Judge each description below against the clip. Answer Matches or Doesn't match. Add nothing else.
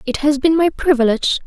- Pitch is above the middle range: Matches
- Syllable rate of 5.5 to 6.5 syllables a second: Matches